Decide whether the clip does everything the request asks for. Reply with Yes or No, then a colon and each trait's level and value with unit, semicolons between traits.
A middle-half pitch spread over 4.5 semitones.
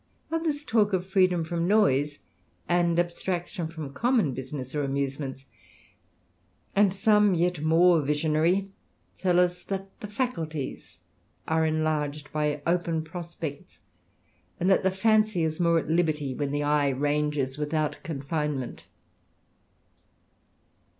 No: average, 3.7 semitones